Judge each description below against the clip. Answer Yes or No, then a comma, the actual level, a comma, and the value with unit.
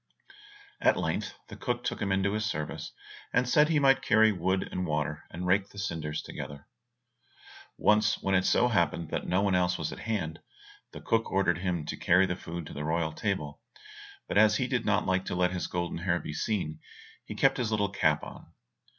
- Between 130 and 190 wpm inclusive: No, fast, 205 wpm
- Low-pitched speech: Yes, very low, 95 Hz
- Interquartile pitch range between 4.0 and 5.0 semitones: Yes, average, 4.3 semitones